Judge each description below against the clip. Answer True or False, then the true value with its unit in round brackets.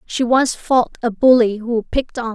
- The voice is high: True (235 Hz)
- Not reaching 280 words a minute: True (205 wpm)